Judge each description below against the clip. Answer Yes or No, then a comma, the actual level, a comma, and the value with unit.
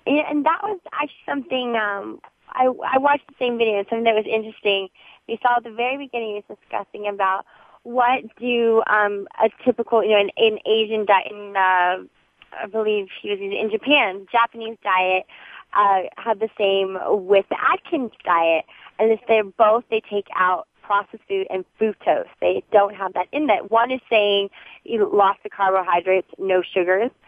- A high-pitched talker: Yes, high, 220 Hz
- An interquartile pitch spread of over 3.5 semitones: No, average, 3.2 semitones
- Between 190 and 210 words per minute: No, average, 180 wpm